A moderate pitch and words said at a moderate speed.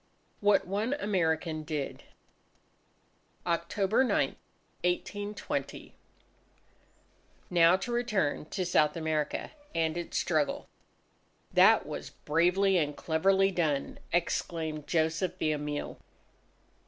No: medium, 170 Hz; slow, 90 wpm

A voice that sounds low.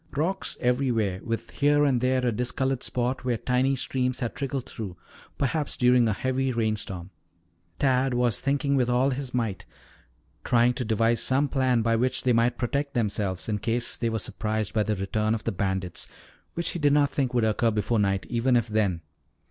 Yes: low, 120 Hz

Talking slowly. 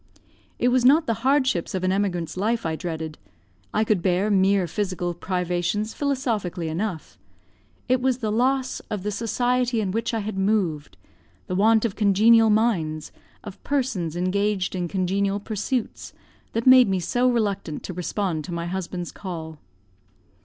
No: average, 155 wpm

